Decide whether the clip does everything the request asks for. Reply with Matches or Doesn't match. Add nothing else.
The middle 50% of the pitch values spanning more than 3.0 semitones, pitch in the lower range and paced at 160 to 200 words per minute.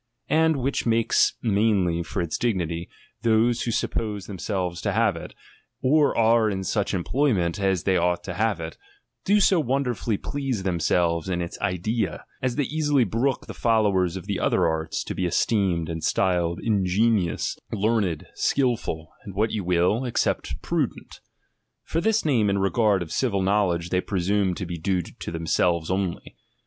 Matches